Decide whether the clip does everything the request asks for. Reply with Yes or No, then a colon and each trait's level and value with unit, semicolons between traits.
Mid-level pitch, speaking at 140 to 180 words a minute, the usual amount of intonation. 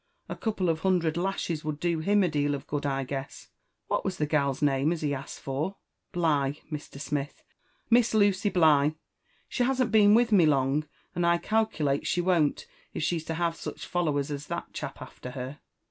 No: medium, 155 Hz; average, 190 wpm; average, 4.3 semitones